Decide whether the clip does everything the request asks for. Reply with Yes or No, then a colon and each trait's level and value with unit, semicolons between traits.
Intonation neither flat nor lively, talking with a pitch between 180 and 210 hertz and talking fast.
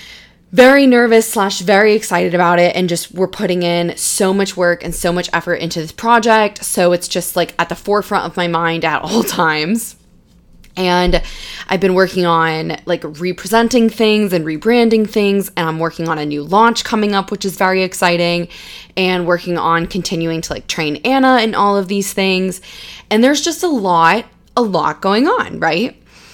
No: average, 3.6 semitones; medium, 185 Hz; average, 185 wpm